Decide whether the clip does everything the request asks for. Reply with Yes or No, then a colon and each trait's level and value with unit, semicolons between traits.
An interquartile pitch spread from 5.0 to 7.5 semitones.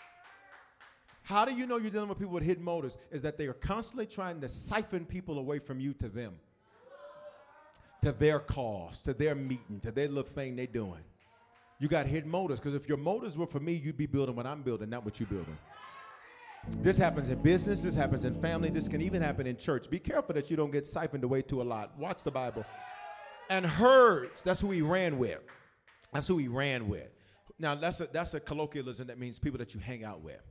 Yes: average, 5.3 semitones